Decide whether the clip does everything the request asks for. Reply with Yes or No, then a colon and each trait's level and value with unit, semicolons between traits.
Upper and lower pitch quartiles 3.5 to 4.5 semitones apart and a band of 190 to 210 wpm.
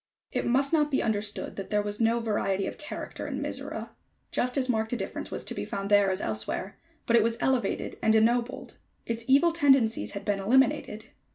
Yes: average, 3.8 semitones; average, 200 wpm